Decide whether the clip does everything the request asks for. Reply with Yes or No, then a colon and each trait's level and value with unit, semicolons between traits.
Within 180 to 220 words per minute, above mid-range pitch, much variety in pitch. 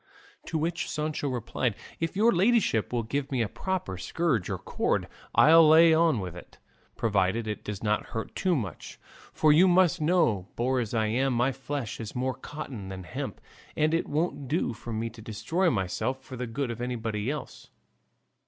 No: average, 185 wpm; low, 130 Hz; wide, 6.2 semitones